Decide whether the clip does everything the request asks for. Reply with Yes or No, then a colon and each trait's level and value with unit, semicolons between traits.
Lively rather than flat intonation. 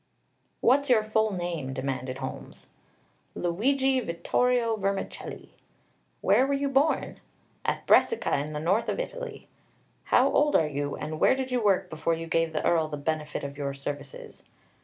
Yes: wide, 8.9 semitones